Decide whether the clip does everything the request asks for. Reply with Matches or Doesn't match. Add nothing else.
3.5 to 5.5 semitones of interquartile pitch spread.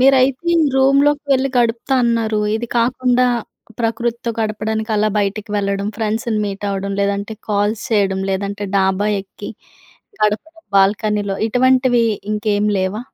Doesn't match